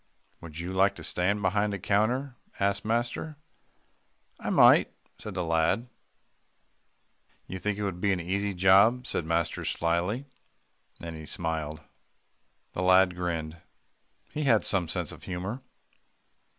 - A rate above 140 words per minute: No, slow, 135 wpm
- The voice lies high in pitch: No, very low, 95 Hz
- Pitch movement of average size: Yes, average, 3.5 semitones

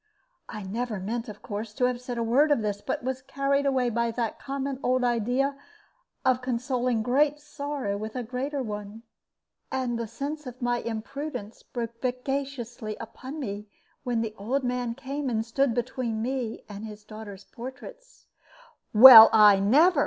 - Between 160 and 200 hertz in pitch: No, high, 245 Hz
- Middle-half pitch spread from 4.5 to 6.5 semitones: No, average, 3.3 semitones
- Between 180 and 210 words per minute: No, average, 165 wpm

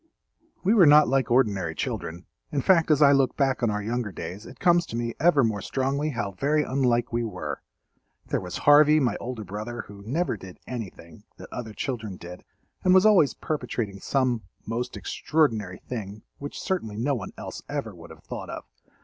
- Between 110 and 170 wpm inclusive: No, average, 185 wpm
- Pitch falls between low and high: No, low, 120 Hz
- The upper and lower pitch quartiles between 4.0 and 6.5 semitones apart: Yes, wide, 5.6 semitones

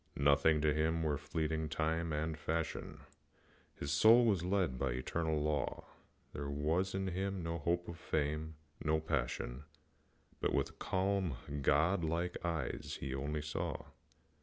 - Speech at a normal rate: Yes, average, 145 wpm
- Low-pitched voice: Yes, very low, 80 Hz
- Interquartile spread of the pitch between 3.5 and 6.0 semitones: No, narrow, 2.5 semitones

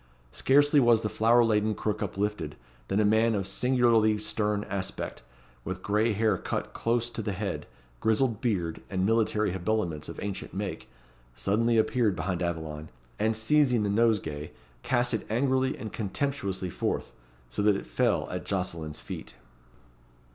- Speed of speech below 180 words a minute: Yes, average, 150 wpm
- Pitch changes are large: No, average, 3.4 semitones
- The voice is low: Yes, low, 105 Hz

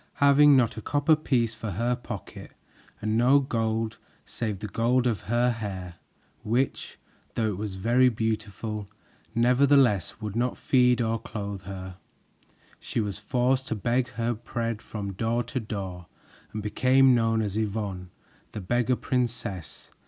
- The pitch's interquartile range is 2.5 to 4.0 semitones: Yes, average, 2.9 semitones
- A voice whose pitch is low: Yes, low, 115 Hz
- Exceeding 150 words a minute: No, average, 145 wpm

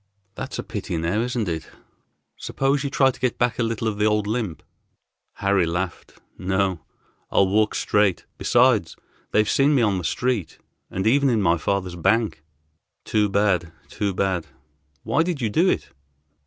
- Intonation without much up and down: No, average, 4.5 semitones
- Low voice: Yes, low, 105 Hz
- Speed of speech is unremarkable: Yes, average, 170 wpm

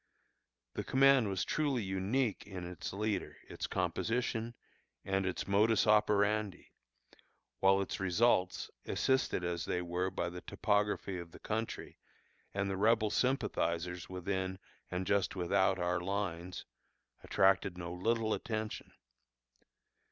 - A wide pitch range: No, average, 3.1 semitones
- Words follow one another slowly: Yes, slow, 120 wpm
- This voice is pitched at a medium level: No, very low, 95 Hz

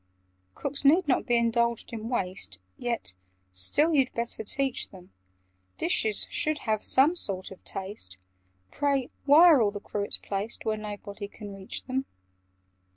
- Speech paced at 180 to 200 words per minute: No, average, 150 wpm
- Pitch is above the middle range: Yes, high, 225 Hz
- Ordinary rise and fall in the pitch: Yes, average, 4.9 semitones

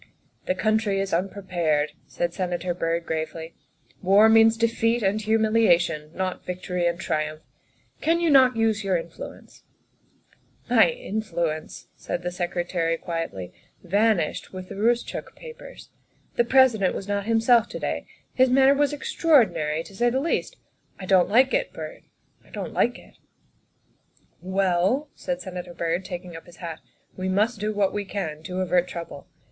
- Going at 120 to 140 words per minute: No, average, 175 wpm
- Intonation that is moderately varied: Yes, average, 4.5 semitones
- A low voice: No, high, 190 Hz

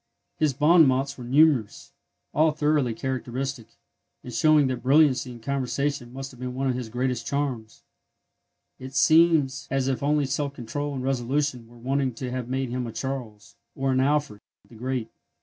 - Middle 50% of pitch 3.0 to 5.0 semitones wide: No, narrow, 2.4 semitones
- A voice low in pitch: Yes, low, 130 Hz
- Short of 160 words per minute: No, average, 170 wpm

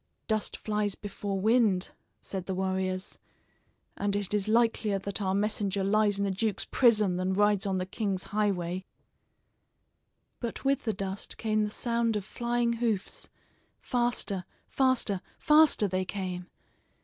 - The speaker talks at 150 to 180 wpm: No, average, 140 wpm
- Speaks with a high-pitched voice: Yes, high, 205 Hz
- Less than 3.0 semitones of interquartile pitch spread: Yes, narrow, 2.6 semitones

